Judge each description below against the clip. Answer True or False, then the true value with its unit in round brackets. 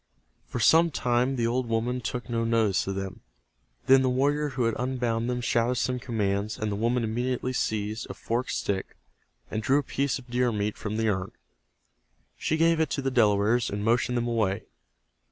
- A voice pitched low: True (120 Hz)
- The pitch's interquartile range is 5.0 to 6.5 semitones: False (2.7 semitones)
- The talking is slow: False (190 wpm)